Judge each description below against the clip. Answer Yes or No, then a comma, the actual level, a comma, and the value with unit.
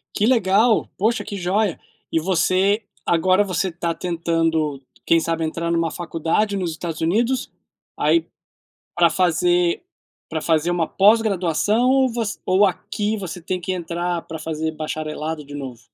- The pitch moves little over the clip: No, average, 3.6 semitones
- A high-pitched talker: No, medium, 175 Hz